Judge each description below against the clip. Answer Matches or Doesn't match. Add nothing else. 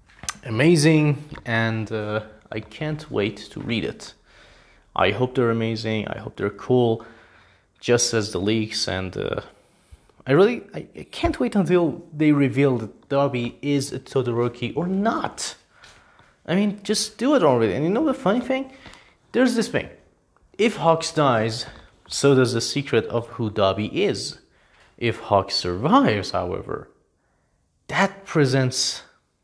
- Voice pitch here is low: Matches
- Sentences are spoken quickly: Doesn't match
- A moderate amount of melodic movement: Doesn't match